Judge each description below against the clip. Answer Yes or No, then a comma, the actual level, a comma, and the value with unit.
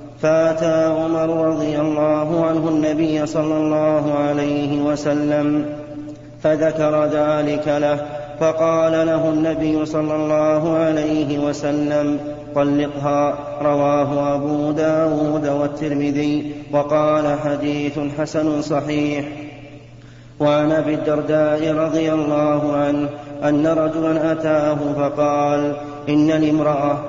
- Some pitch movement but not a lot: No, narrow, 1.0 semitones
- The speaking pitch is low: No, medium, 150 Hz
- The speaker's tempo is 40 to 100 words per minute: Yes, average, 90 wpm